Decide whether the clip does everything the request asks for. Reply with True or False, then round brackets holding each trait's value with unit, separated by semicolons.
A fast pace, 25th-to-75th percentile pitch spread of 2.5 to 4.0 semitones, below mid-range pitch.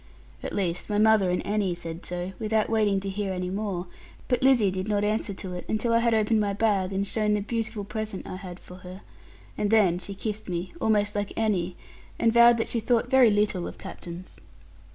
False (215 wpm; 2.8 semitones; 205 Hz)